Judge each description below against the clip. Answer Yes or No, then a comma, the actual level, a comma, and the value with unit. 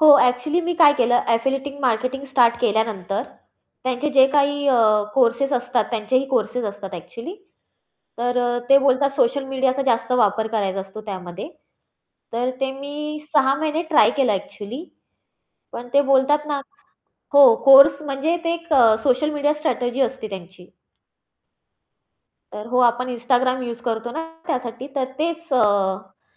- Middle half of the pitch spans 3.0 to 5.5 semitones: Yes, average, 3.5 semitones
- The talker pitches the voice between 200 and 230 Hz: No, very high, 255 Hz